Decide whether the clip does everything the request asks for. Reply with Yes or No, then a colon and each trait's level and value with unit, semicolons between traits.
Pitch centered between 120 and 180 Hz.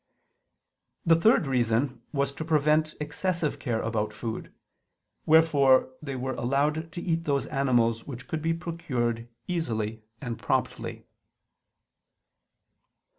Yes: medium, 140 Hz